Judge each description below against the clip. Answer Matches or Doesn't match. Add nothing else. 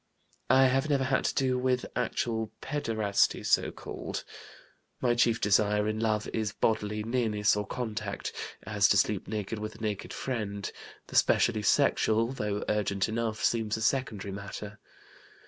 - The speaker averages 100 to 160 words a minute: Matches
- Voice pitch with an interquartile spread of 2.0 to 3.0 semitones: Matches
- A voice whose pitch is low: Matches